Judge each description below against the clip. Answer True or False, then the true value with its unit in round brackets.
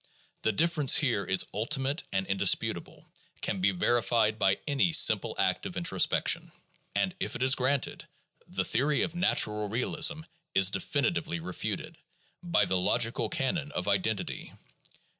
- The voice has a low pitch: True (115 Hz)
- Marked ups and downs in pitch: True (6.4 semitones)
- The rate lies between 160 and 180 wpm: False (140 wpm)